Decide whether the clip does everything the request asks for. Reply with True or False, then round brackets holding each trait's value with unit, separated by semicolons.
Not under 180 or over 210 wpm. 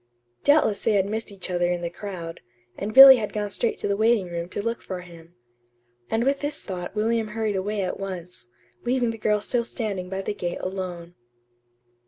True (200 wpm)